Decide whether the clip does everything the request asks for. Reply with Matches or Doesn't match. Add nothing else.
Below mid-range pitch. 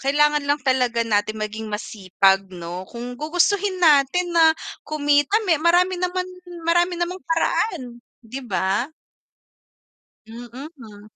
Doesn't match